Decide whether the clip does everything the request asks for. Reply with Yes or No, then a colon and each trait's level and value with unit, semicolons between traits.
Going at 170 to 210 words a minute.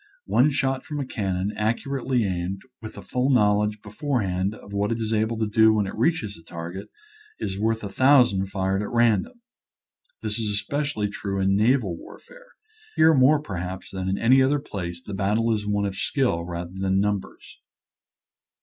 Yes: average, 190 wpm